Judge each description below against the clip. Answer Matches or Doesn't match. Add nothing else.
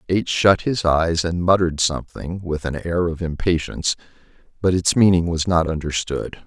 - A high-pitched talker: Doesn't match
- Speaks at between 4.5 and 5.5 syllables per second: Matches